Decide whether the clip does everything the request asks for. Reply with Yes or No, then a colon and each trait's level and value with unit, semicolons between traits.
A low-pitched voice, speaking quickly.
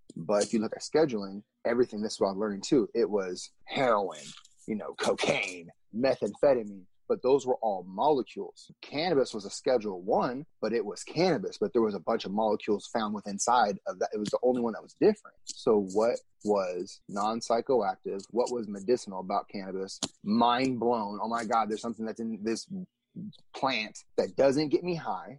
No: low, 115 Hz; average, 185 wpm